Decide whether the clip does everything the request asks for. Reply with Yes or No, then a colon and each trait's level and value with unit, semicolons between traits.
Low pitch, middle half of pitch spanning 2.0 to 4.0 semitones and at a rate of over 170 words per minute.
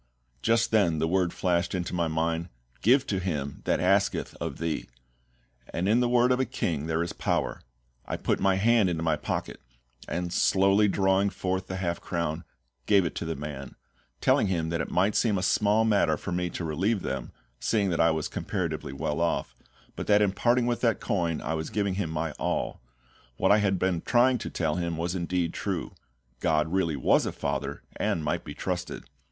Yes: very low, 90 Hz; average, 3.7 semitones; average, 200 wpm